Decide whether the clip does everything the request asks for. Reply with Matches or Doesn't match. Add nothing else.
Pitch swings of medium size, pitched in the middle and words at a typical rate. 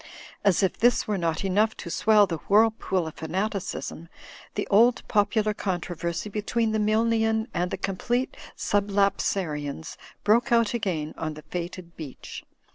Doesn't match